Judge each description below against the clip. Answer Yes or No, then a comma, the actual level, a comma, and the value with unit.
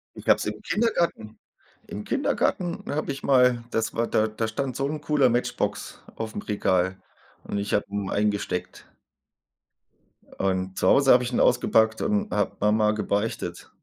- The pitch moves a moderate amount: Yes, average, 4.9 semitones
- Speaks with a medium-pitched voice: No, low, 110 Hz